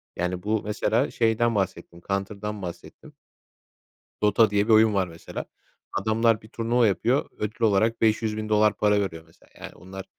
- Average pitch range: No, narrow, 2.3 semitones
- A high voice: No, low, 105 Hz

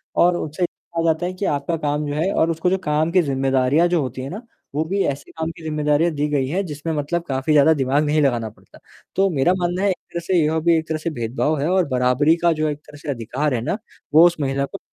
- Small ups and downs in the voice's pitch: No, average, 3.3 semitones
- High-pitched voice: No, medium, 155 Hz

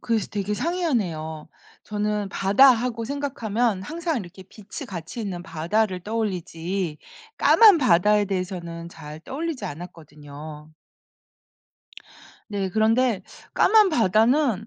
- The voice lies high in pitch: Yes, high, 205 Hz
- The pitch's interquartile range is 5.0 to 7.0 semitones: Yes, wide, 5.4 semitones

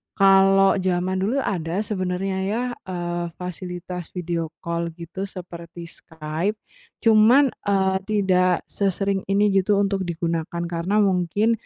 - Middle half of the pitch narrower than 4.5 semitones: Yes, narrow, 2.4 semitones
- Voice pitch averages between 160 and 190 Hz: Yes, medium, 185 Hz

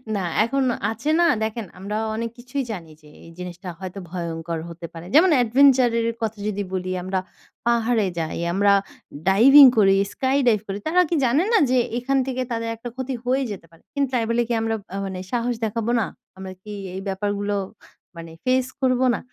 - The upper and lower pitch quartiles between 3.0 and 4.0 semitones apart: No, average, 4.8 semitones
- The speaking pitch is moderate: No, high, 225 Hz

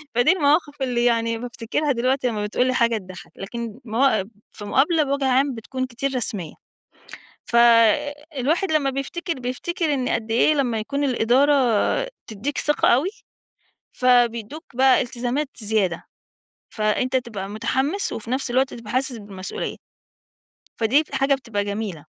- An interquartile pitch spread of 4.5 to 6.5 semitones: No, average, 3.6 semitones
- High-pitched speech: Yes, very high, 250 Hz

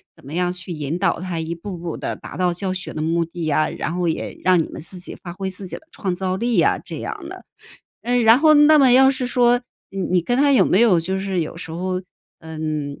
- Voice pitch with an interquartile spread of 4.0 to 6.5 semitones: Yes, average, 5.0 semitones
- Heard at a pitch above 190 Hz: No, medium, 185 Hz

